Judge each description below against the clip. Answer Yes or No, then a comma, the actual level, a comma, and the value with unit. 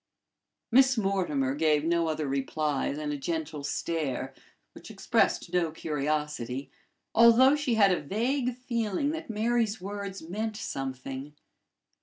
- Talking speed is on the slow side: Yes, slow, 125 wpm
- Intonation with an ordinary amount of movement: No, wide, 7.2 semitones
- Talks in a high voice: No, medium, 170 Hz